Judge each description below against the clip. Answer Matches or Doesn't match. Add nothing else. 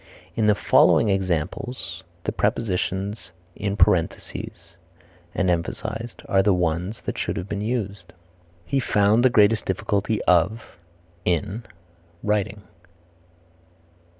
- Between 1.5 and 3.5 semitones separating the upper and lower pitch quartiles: Matches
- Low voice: Matches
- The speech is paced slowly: Matches